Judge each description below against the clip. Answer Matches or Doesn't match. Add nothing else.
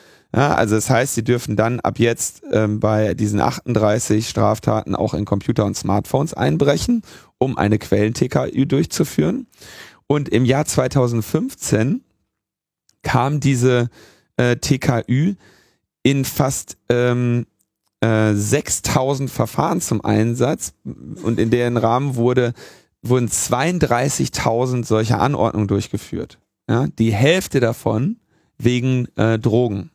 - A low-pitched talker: Matches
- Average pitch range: Matches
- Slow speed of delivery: Matches